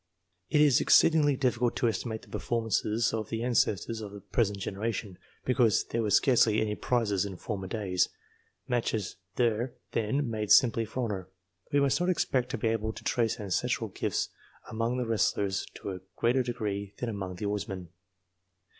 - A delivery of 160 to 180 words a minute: Yes, average, 170 wpm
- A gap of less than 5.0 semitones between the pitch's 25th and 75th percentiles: Yes, average, 3.1 semitones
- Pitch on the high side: No, low, 110 Hz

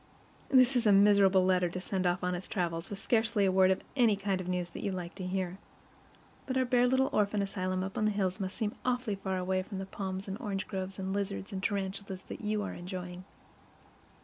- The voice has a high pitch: Yes, high, 195 Hz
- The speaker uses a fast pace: Yes, fast, 230 wpm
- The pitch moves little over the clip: Yes, narrow, 1.9 semitones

